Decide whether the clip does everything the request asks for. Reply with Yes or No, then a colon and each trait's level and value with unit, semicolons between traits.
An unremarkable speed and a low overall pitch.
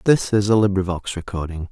Yes: average, 175 wpm; low, 100 Hz